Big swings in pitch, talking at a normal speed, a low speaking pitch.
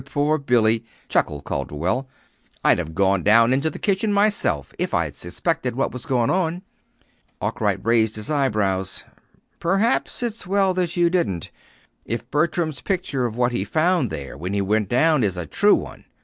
Yes: wide, 8.7 semitones; average, 165 wpm; low, 125 Hz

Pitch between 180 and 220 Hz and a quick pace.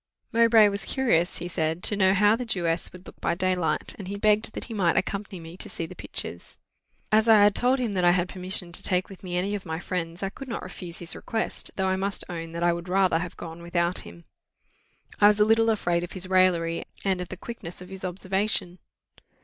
Yes: medium, 185 Hz; fast, 235 wpm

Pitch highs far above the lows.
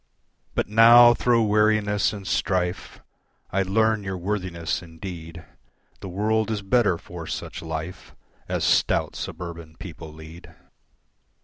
No: average, 4.2 semitones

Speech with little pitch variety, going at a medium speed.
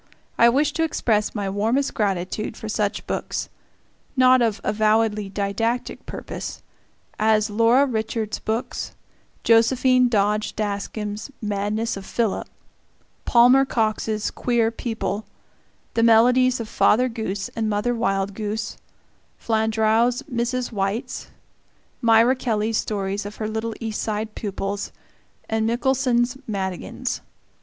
No: narrow, 2.3 semitones; slow, 115 wpm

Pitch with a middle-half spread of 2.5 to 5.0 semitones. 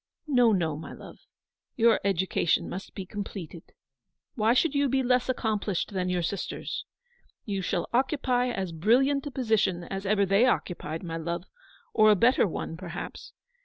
No: wide, 5.6 semitones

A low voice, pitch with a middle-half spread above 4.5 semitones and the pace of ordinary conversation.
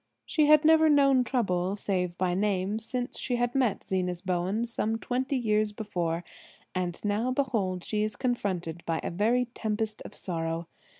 No: high, 210 Hz; average, 5.2 semitones; average, 160 wpm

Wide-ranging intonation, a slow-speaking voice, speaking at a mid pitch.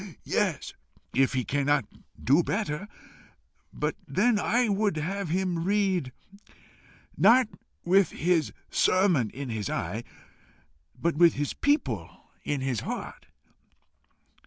Yes: wide, 6.7 semitones; slow, 110 wpm; medium, 170 Hz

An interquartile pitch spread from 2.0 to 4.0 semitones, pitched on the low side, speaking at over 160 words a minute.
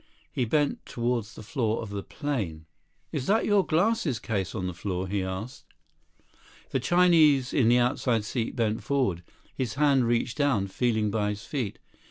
No: average, 5.2 semitones; low, 120 Hz; average, 170 wpm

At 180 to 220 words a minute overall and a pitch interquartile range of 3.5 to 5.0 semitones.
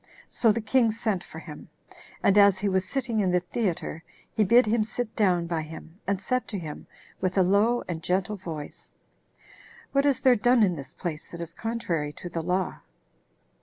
Yes: average, 195 wpm; average, 4.7 semitones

